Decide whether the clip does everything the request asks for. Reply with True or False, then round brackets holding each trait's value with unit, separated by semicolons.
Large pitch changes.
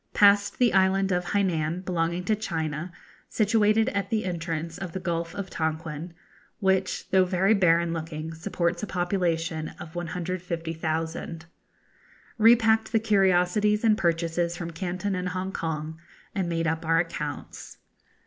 False (3.0 semitones)